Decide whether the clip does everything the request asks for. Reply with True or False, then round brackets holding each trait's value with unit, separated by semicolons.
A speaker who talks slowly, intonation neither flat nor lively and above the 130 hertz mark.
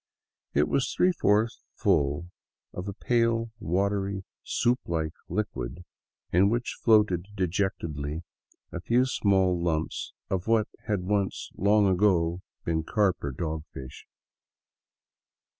False (120 wpm; 4.2 semitones; 95 Hz)